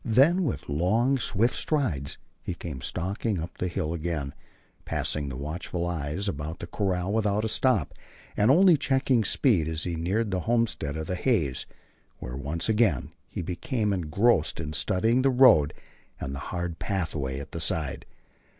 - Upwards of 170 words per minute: No, average, 165 wpm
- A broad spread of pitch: Yes, wide, 6.6 semitones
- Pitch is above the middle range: No, very low, 90 Hz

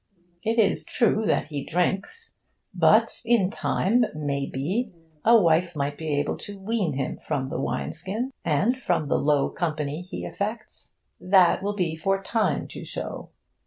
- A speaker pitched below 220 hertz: Yes, medium, 185 Hz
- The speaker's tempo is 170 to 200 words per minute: No, average, 160 wpm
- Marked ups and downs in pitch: Yes, wide, 6.4 semitones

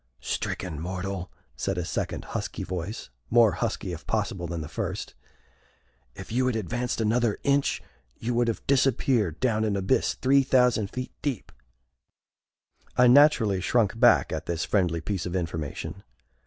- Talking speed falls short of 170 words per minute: Yes, average, 150 wpm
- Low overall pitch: Yes, low, 105 Hz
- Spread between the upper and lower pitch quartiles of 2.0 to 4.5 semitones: No, average, 5.2 semitones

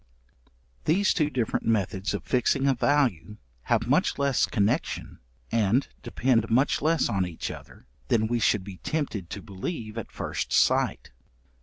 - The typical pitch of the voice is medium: No, low, 115 Hz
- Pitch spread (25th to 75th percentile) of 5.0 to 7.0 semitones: Yes, wide, 5.4 semitones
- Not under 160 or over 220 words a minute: No, average, 150 wpm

